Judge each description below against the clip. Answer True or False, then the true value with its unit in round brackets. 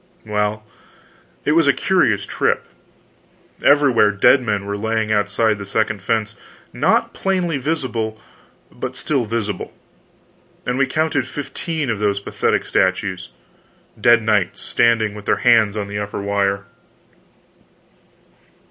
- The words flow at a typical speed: False (125 wpm)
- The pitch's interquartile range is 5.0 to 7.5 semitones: False (4.1 semitones)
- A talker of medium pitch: False (110 Hz)